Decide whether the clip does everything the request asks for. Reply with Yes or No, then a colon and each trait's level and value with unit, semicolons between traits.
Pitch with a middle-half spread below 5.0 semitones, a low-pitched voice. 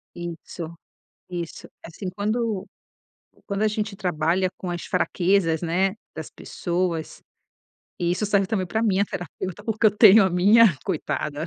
No: average, 3.2 semitones; medium, 185 Hz